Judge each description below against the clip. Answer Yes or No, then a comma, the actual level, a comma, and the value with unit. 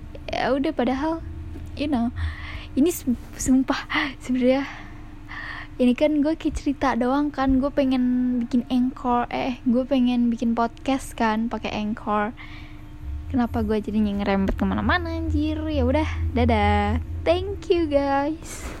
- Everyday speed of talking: Yes, average, 120 wpm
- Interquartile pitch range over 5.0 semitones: Yes, wide, 5.4 semitones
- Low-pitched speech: No, high, 245 Hz